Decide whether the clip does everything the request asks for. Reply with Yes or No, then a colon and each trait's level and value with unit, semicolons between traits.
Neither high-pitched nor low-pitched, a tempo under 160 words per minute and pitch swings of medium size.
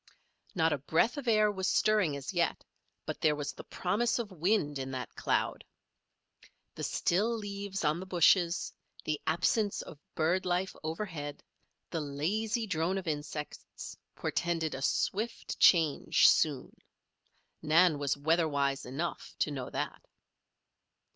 Yes: medium, 170 Hz; average, 140 wpm; average, 4.7 semitones